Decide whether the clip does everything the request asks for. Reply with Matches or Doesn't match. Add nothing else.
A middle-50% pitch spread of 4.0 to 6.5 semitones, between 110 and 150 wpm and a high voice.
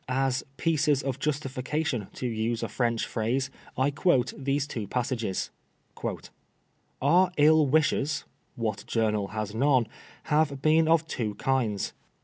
Doesn't match